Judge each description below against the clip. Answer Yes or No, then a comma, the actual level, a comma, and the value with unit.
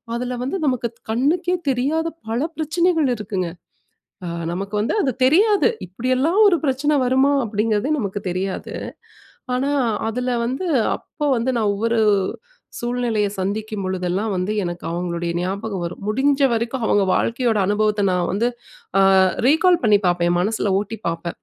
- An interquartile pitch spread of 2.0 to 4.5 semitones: No, average, 5.1 semitones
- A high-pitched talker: Yes, high, 225 Hz